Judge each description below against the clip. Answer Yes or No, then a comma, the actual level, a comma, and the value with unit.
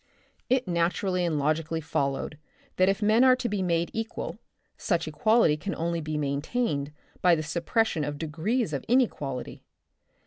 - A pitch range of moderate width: No, wide, 6.3 semitones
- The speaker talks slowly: No, average, 150 wpm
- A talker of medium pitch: Yes, medium, 170 Hz